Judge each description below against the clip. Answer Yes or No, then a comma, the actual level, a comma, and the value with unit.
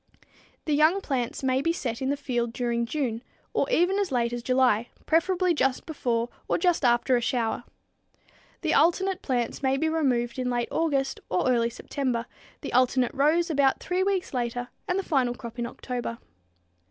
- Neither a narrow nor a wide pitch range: Yes, average, 4.8 semitones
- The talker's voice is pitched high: Yes, very high, 260 Hz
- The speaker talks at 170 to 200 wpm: Yes, average, 180 wpm